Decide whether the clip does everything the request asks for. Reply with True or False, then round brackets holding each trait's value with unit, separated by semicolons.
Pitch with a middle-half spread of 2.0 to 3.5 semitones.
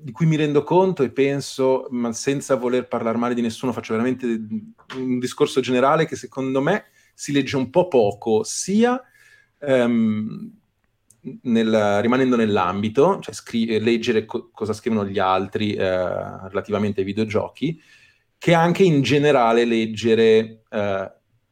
False (3.9 semitones)